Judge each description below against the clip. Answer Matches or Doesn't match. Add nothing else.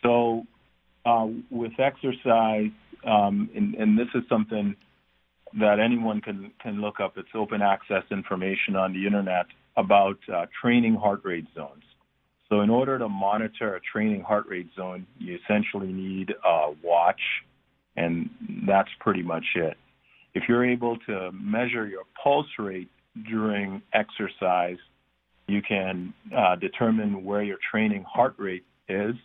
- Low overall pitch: Matches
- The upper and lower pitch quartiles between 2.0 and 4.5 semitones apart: Matches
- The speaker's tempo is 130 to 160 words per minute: Matches